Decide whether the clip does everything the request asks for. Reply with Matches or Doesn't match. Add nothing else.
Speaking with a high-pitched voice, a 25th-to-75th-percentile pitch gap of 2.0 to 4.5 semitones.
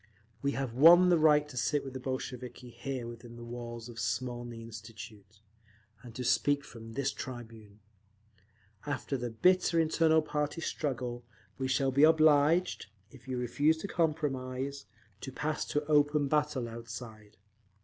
Doesn't match